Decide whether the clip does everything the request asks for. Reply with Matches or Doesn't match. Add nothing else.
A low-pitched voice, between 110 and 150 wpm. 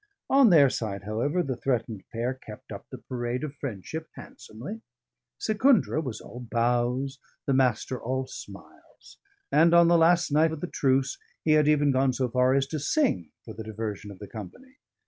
Doesn't match